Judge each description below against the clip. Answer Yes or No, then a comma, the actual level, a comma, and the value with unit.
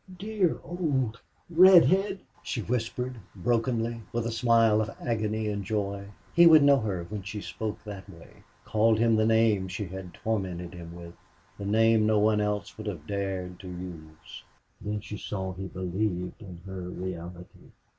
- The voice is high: No, low, 105 Hz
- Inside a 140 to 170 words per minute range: Yes, average, 165 wpm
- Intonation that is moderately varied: Yes, average, 3.6 semitones